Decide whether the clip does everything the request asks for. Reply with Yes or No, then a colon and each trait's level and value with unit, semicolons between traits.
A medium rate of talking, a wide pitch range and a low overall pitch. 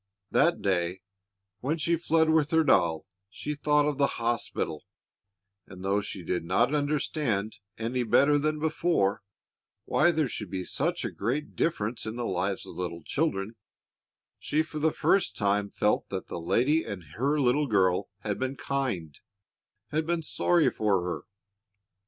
Yes: average, 155 wpm; wide, 7.6 semitones; low, 120 Hz